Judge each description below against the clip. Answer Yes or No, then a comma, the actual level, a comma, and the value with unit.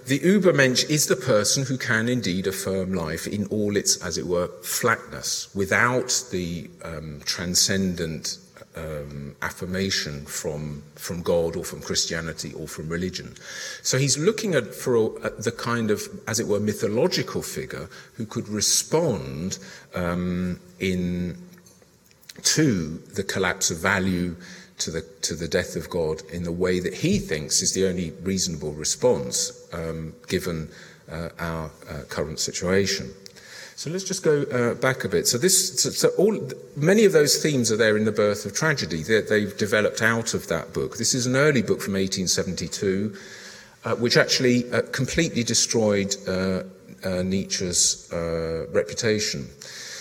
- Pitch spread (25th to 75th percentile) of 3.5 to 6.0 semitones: Yes, wide, 5.4 semitones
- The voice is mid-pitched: No, very low, 95 Hz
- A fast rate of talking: No, average, 155 wpm